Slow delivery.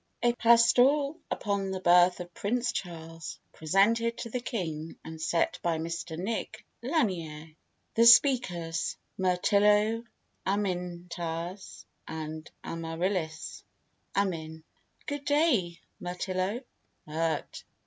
Yes: slow, 95 wpm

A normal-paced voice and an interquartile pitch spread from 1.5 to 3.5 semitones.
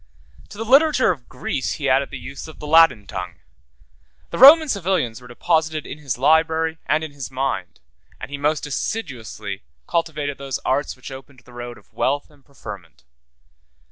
No: average, 175 wpm; average, 4.1 semitones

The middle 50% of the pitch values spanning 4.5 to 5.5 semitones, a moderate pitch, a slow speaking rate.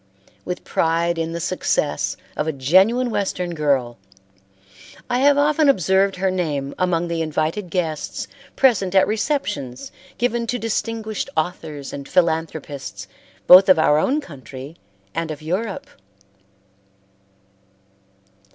Yes: average, 5.2 semitones; medium, 175 Hz; slow, 120 wpm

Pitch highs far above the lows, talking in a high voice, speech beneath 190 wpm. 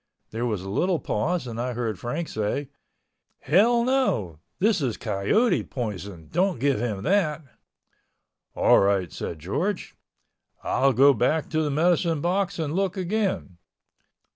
No: wide, 8.9 semitones; medium, 145 Hz; average, 140 wpm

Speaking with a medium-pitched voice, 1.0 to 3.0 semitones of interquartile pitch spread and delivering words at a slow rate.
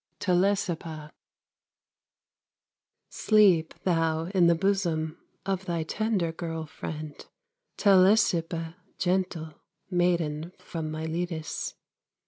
Yes: medium, 170 Hz; average, 2.7 semitones; slow, 80 wpm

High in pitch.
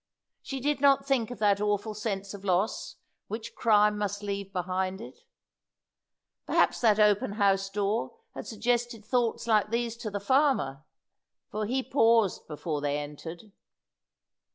Yes: high, 210 Hz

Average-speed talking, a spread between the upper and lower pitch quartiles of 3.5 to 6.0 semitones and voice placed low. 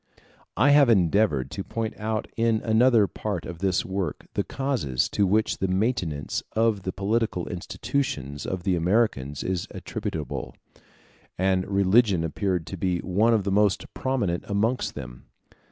Yes: average, 150 wpm; average, 4.0 semitones; low, 100 Hz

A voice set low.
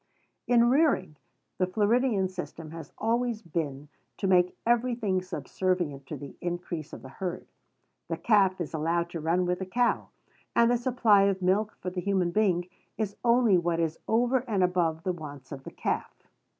No: medium, 185 Hz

